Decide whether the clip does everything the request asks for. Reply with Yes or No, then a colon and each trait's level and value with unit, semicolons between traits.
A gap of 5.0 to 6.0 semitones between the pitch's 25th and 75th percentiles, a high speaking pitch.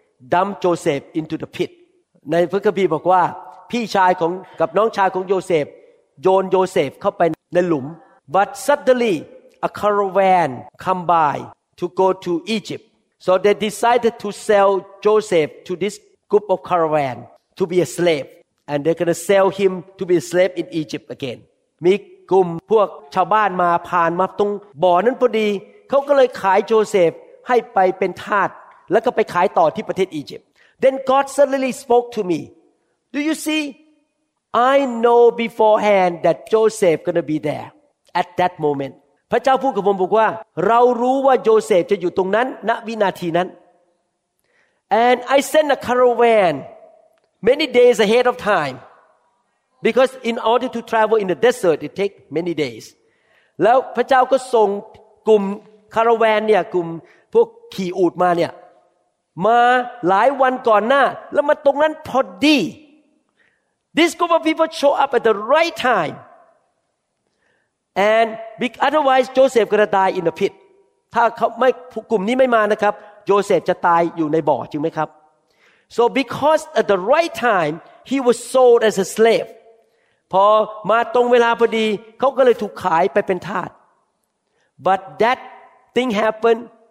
Yes: wide, 5.5 semitones; high, 215 Hz